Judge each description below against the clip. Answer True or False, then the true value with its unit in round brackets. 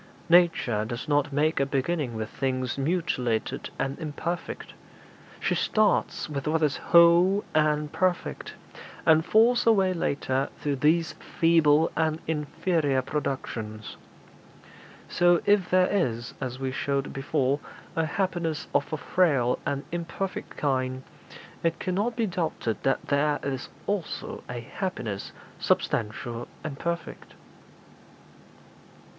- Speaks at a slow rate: True (120 wpm)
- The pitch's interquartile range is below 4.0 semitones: False (4.4 semitones)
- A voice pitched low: False (150 Hz)